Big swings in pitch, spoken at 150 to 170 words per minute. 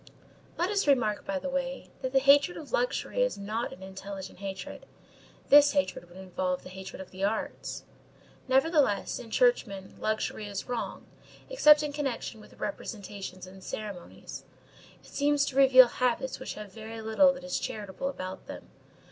Yes: wide, 6.2 semitones; average, 165 wpm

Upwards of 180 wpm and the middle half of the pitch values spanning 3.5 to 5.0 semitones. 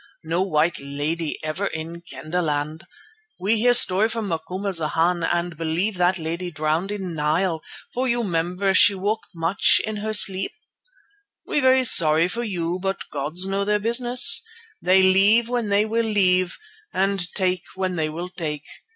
No: average, 155 wpm; average, 3.9 semitones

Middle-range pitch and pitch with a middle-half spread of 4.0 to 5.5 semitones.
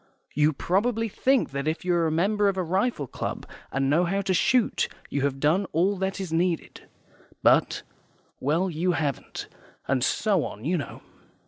Yes: medium, 175 Hz; average, 4.5 semitones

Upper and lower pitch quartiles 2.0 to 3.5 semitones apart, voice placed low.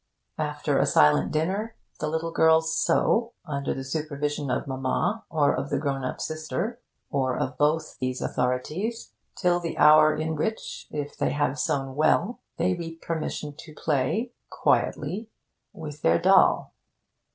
No: average, 3.2 semitones; medium, 155 Hz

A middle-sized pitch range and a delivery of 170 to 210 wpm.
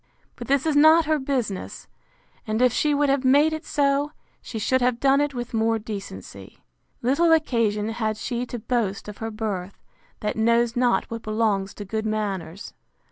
Yes: average, 4.4 semitones; average, 180 wpm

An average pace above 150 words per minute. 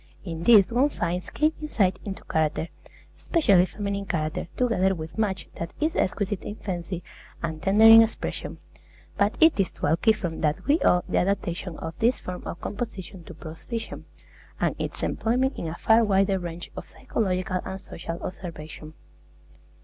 Yes: average, 165 wpm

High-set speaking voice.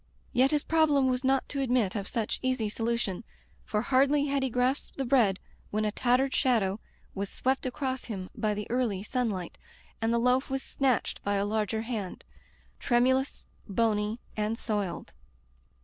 Yes: high, 240 Hz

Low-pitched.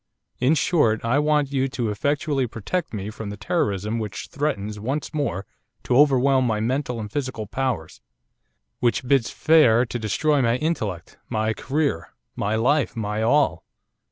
Yes: low, 125 Hz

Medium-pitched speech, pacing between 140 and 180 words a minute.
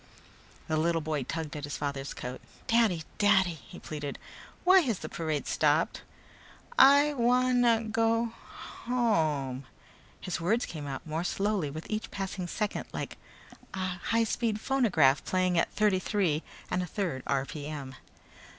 Yes: medium, 180 Hz; average, 145 wpm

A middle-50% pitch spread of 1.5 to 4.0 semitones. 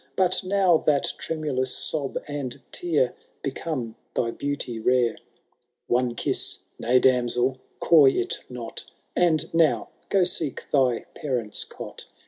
No: average, 4.4 semitones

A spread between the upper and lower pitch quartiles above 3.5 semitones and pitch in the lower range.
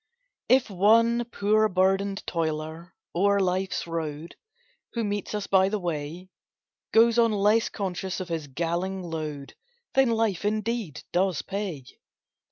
No: average, 4.0 semitones; high, 190 Hz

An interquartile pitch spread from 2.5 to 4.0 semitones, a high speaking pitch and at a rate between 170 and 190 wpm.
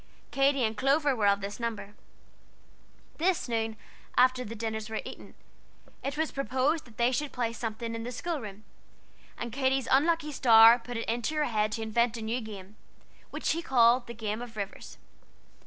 Yes: average, 3.4 semitones; high, 235 Hz; average, 180 wpm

